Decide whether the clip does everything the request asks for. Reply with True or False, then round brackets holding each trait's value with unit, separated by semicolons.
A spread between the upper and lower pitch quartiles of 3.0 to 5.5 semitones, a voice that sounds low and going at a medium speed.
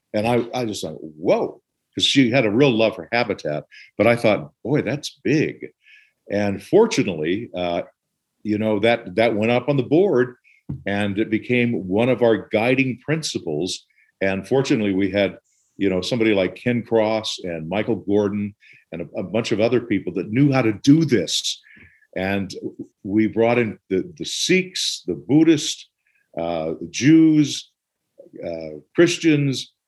True (4.2 semitones; 110 Hz; 160 wpm)